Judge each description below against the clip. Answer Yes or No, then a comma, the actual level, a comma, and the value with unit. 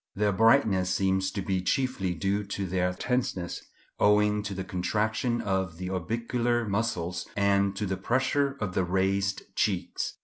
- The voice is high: No, low, 100 Hz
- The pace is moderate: Yes, average, 150 wpm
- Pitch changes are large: No, average, 2.9 semitones